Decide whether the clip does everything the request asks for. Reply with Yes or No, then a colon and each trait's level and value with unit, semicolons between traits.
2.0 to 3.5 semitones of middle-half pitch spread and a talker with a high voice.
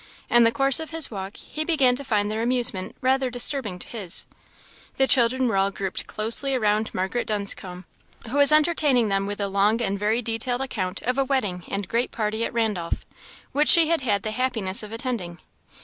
No: average, 4.5 semitones; high, 230 Hz